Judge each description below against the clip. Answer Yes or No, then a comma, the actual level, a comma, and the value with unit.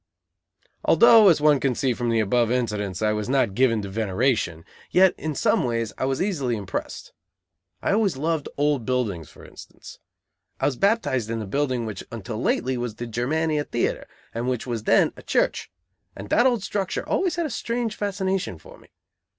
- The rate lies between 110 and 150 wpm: No, average, 185 wpm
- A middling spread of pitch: No, wide, 6.3 semitones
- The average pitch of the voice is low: Yes, low, 125 Hz